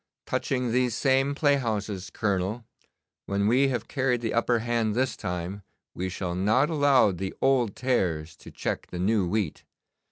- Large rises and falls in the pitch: No, average, 4.9 semitones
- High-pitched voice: No, low, 110 Hz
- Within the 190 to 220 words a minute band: No, average, 155 wpm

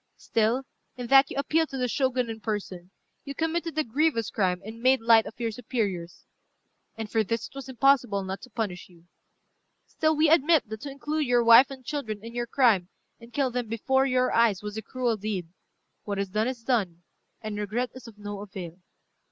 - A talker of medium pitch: No, high, 230 Hz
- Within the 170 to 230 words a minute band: Yes, average, 200 wpm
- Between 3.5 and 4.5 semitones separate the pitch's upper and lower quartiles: Yes, average, 4.1 semitones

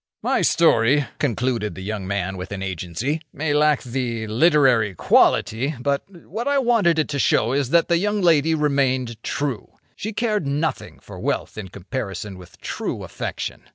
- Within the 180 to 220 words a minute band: No, average, 165 wpm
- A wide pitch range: Yes, wide, 6.5 semitones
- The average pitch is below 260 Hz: Yes, low, 135 Hz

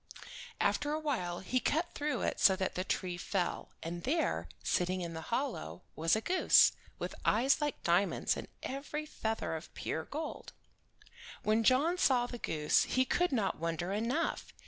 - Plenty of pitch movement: Yes, wide, 8.6 semitones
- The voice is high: Yes, high, 225 Hz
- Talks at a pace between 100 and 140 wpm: No, average, 165 wpm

